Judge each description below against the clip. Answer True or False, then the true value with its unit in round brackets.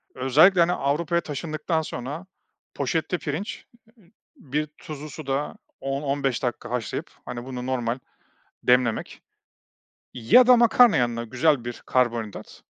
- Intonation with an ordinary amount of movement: True (4.3 semitones)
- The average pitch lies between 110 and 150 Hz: True (140 Hz)